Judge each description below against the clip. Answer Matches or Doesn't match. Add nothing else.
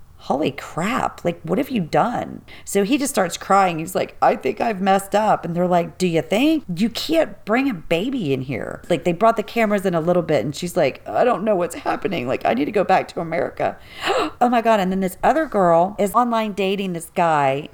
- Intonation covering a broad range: Doesn't match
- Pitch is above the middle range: Matches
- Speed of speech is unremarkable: Doesn't match